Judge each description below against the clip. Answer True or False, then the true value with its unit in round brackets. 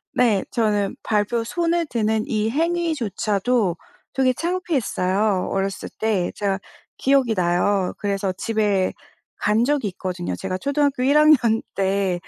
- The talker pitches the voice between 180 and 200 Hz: False (215 Hz)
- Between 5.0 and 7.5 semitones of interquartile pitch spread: True (5.4 semitones)